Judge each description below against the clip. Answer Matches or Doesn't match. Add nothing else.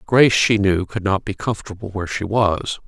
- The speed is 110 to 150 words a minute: Doesn't match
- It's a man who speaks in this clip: Matches